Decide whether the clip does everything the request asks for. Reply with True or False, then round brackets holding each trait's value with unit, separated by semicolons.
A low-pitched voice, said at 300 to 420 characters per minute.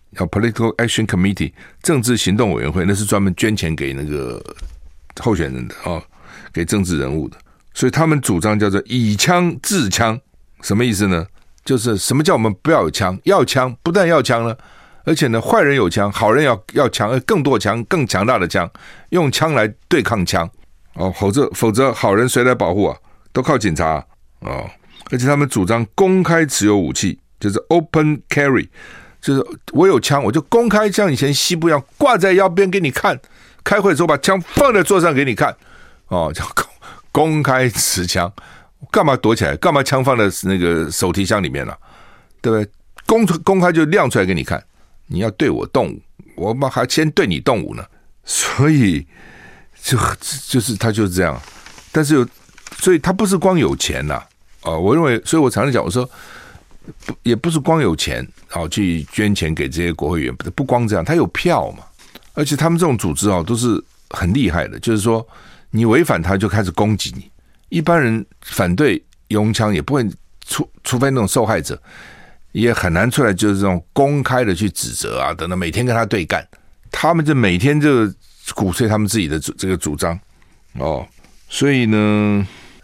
False (115 Hz; 290 characters per minute)